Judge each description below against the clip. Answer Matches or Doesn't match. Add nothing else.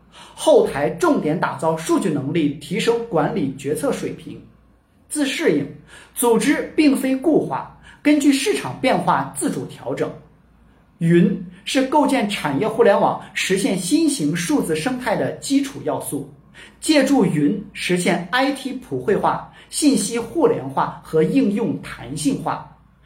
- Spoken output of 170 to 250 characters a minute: Matches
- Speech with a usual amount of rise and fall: Doesn't match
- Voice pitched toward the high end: Matches